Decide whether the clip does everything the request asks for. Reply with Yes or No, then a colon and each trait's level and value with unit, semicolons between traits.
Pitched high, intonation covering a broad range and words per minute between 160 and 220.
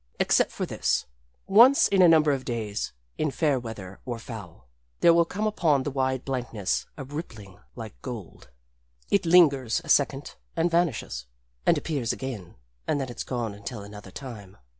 No: low, 130 Hz; wide, 6.4 semitones; average, 165 wpm